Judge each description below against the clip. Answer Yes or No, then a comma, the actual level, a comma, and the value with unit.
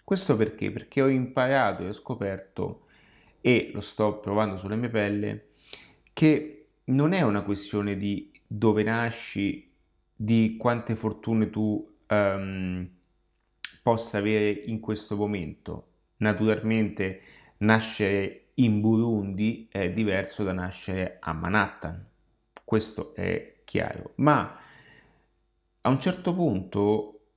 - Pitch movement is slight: Yes, narrow, 2.3 semitones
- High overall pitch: No, low, 105 Hz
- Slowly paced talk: Yes, slow, 110 wpm